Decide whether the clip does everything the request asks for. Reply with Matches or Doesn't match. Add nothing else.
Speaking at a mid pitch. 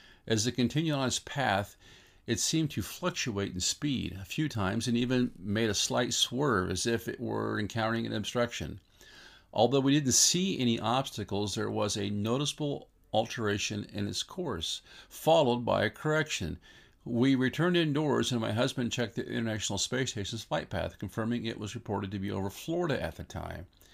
Doesn't match